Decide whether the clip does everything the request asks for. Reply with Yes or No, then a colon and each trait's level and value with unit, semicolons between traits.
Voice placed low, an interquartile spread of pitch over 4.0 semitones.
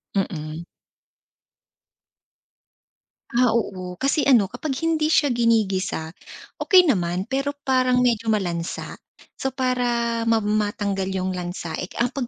No: high, 230 Hz; average, 5.3 semitones